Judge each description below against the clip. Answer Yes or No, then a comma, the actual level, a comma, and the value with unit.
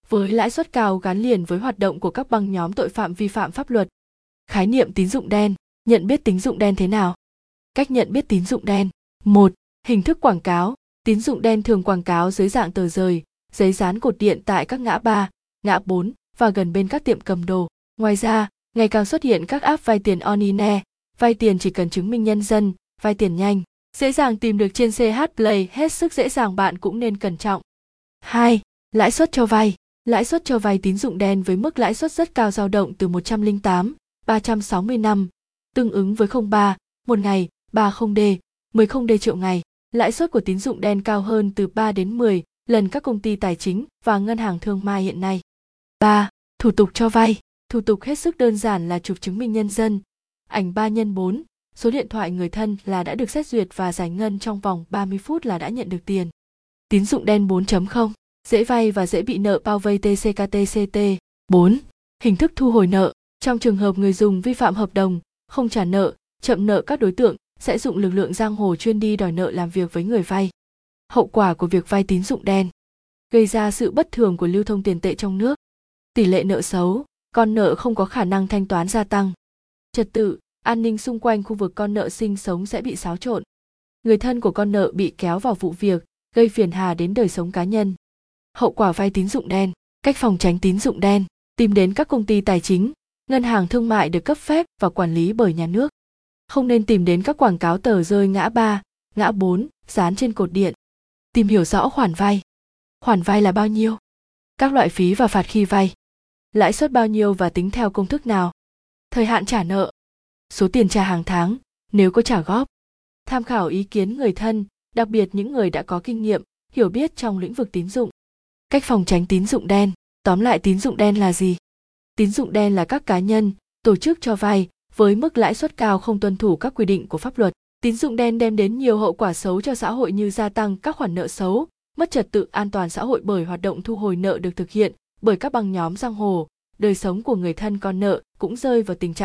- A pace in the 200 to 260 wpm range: Yes, average, 230 wpm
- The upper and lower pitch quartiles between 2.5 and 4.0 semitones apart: Yes, average, 3.3 semitones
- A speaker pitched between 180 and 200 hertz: No, high, 210 Hz